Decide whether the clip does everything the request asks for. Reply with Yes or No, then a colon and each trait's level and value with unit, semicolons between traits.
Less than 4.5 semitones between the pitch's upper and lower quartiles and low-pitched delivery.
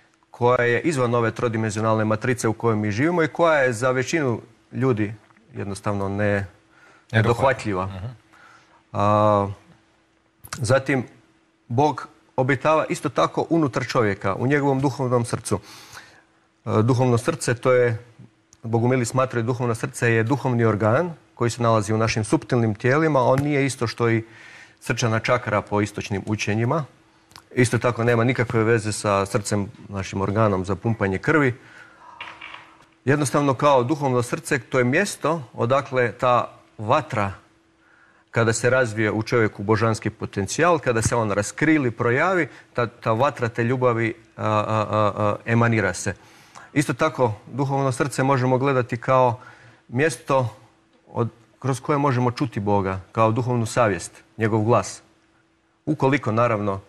Yes: average, 3.3 semitones; low, 120 Hz